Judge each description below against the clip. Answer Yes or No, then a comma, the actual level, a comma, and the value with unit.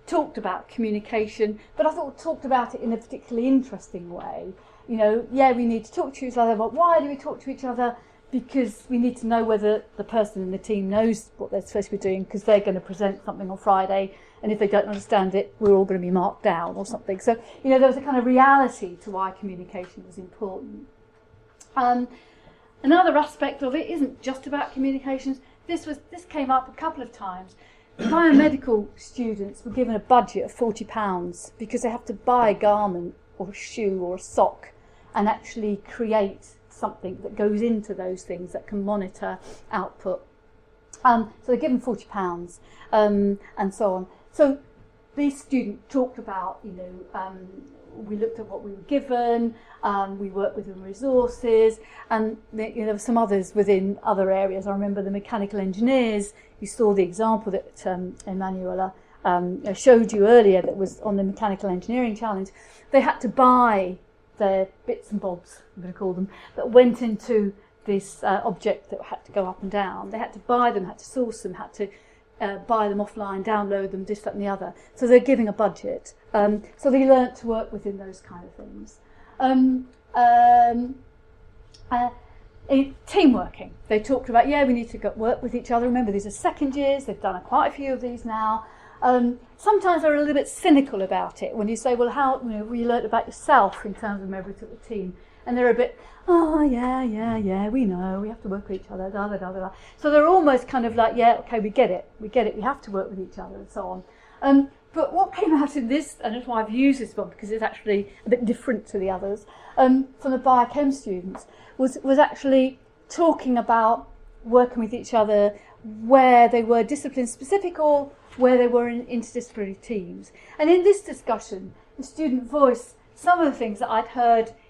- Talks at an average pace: No, fast, 210 wpm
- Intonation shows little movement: No, average, 4.2 semitones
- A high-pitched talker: Yes, high, 225 Hz